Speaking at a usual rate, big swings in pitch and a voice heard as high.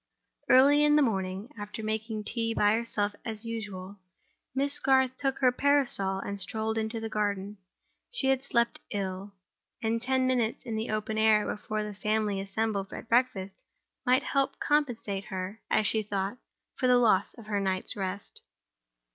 No: average, 165 wpm; average, 3.7 semitones; high, 220 Hz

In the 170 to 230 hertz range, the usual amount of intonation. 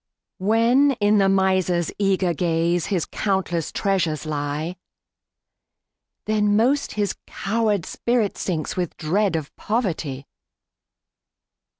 Yes: high, 190 Hz; average, 4.0 semitones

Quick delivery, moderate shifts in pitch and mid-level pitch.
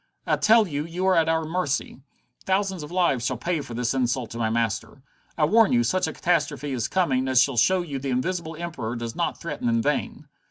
No: fast, 225 wpm; wide, 6.0 semitones; medium, 145 Hz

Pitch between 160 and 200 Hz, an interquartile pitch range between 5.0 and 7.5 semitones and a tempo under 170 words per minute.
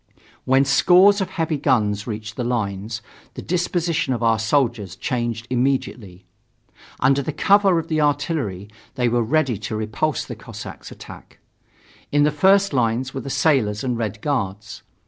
No: low, 130 Hz; wide, 5.5 semitones; average, 150 wpm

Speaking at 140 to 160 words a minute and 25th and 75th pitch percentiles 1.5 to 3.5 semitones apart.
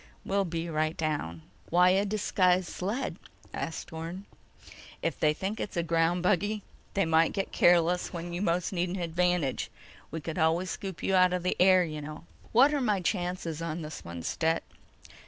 No: average, 175 wpm; narrow, 2.5 semitones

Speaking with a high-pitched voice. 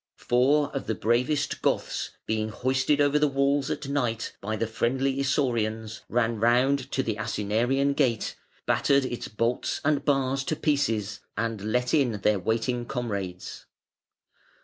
No: low, 125 Hz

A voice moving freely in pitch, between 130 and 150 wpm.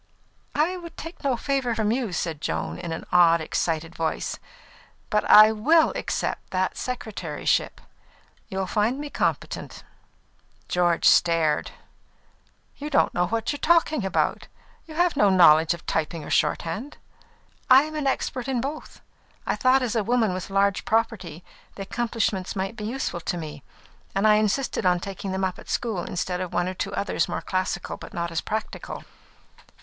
No: wide, 6.3 semitones; average, 165 wpm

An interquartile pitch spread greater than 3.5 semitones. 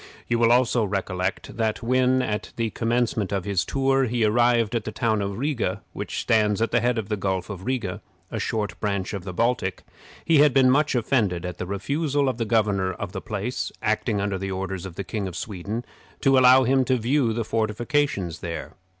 Yes: average, 4.2 semitones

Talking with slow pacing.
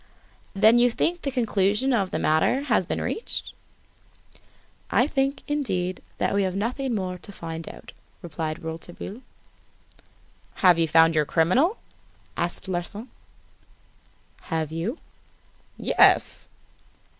Yes: slow, 120 wpm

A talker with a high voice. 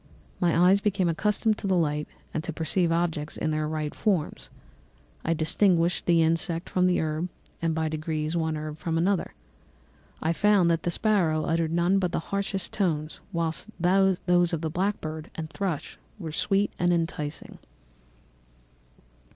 No: medium, 165 Hz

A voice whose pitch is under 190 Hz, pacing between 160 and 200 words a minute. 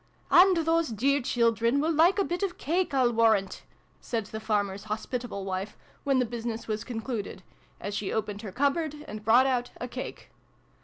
No: high, 240 Hz; average, 185 wpm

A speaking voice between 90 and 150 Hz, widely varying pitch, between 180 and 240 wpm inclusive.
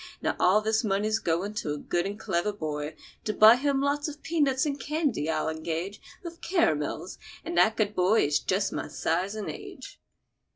No: high, 210 Hz; wide, 8.1 semitones; average, 190 wpm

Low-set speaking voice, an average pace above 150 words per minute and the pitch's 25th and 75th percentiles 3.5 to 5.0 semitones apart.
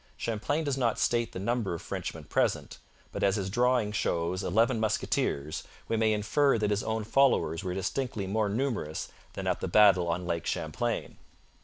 Yes: low, 105 Hz; average, 175 wpm; average, 4.0 semitones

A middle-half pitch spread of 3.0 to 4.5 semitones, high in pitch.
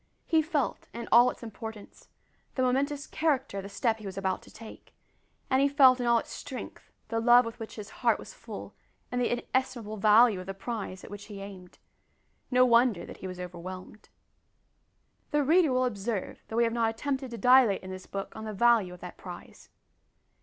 Yes: average, 4.2 semitones; high, 230 Hz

